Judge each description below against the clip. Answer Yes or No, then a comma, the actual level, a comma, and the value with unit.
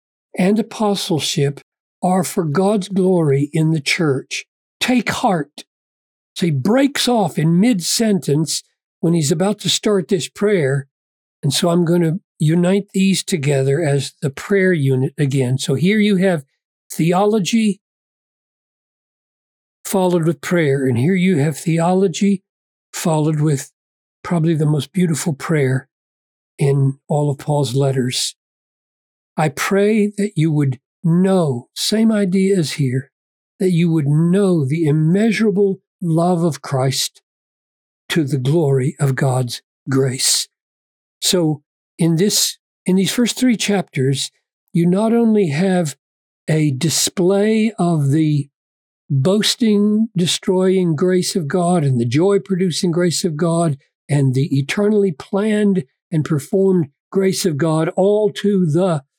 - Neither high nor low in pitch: Yes, medium, 170 Hz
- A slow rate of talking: Yes, slow, 130 wpm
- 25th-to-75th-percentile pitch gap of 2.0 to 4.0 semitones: No, wide, 5.5 semitones